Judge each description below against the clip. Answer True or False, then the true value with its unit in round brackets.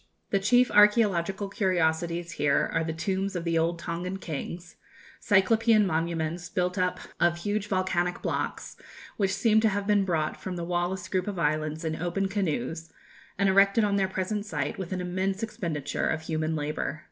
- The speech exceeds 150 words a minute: True (170 wpm)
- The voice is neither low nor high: True (180 Hz)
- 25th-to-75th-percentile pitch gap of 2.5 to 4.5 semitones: True (3.1 semitones)